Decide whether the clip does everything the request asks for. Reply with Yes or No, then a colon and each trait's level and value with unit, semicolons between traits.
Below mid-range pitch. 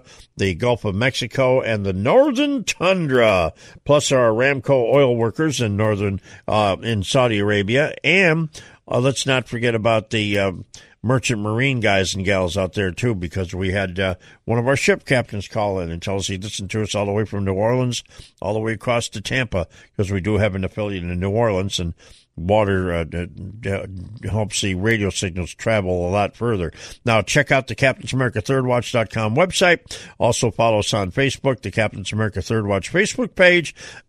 Yes: low, 110 Hz